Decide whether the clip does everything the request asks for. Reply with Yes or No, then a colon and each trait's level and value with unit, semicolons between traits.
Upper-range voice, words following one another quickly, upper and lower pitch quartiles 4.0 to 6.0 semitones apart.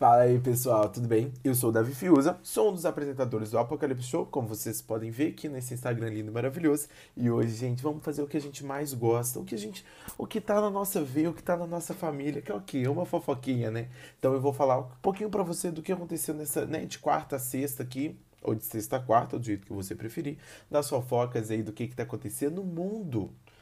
No: low, 135 Hz; fast, 250 wpm; average, 4.8 semitones